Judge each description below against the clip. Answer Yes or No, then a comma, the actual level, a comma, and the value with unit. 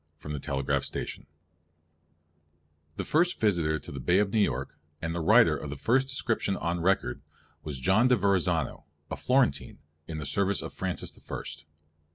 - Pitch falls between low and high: No, very low, 85 Hz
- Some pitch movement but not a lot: Yes, average, 4.7 semitones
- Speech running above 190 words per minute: No, average, 155 wpm